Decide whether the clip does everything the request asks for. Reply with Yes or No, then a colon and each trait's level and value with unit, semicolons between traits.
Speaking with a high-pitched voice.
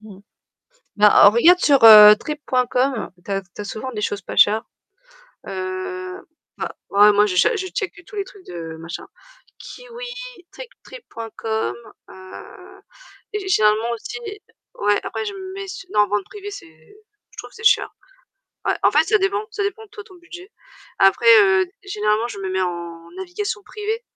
Yes: high, 235 Hz